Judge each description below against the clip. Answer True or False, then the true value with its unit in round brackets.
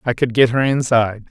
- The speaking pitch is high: False (120 Hz)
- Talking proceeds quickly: True (230 wpm)